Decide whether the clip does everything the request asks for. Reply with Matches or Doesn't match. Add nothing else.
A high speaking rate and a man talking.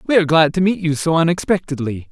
Matches